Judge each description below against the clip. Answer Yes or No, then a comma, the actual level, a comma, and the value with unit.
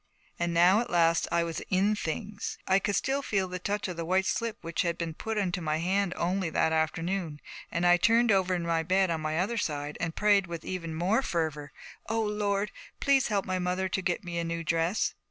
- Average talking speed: No, fast, 225 wpm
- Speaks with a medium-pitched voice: Yes, medium, 180 Hz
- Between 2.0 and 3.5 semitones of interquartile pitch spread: Yes, average, 3.2 semitones